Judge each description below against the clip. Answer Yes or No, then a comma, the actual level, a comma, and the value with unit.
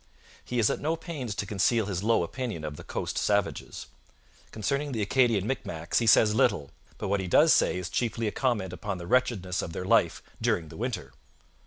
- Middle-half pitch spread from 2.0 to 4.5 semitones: No, average, 5.1 semitones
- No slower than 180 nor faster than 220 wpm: Yes, average, 200 wpm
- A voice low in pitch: Yes, low, 105 Hz